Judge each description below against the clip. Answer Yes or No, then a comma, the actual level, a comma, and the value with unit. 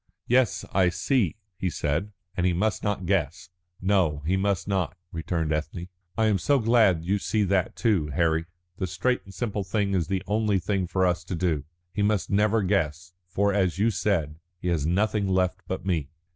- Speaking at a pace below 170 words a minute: No, average, 190 wpm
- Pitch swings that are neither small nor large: Yes, average, 3.1 semitones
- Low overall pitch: Yes, very low, 95 Hz